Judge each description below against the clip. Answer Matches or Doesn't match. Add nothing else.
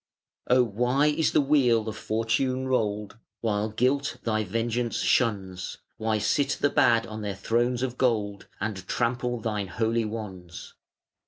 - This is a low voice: Matches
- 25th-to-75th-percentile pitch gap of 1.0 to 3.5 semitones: Matches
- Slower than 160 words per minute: Matches